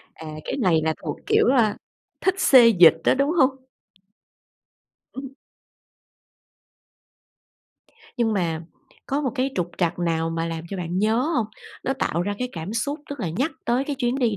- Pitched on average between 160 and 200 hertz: No, high, 230 Hz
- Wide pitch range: Yes, wide, 7.6 semitones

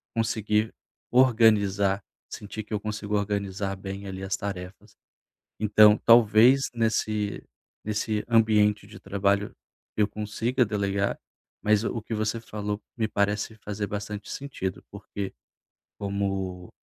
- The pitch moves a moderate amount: No, narrow, 1.4 semitones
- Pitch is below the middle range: Yes, low, 105 Hz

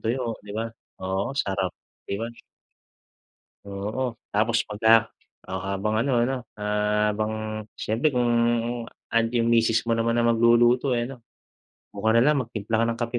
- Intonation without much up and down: Yes, narrow, 2.0 semitones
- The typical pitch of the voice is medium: No, low, 115 Hz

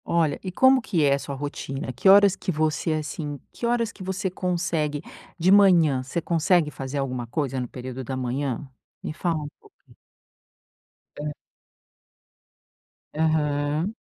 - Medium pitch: Yes, medium, 155 Hz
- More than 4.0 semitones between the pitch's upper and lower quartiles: Yes, average, 4.5 semitones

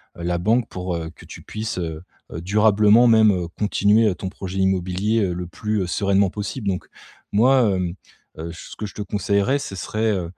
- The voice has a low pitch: Yes, low, 100 Hz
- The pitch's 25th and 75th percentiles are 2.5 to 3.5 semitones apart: Yes, average, 3.0 semitones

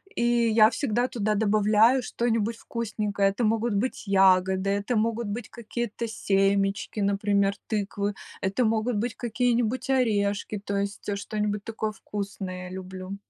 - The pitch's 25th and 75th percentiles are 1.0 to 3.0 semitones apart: Yes, narrow, 2.5 semitones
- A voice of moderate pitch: No, high, 210 Hz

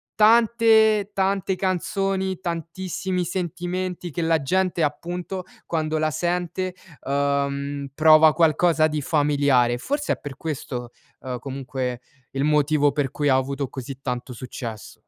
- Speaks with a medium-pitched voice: Yes, medium, 155 Hz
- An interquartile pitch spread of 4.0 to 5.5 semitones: Yes, average, 4.8 semitones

